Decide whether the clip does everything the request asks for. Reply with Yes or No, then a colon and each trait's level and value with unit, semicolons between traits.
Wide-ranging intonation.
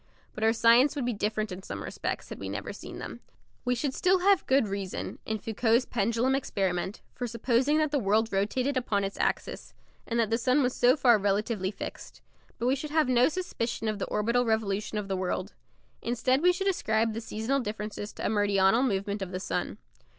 No: average, 3.8 semitones